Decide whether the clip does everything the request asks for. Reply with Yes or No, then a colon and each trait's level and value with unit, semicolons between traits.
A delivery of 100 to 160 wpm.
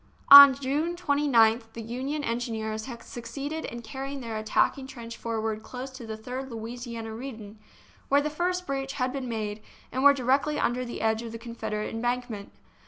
No: average, 175 wpm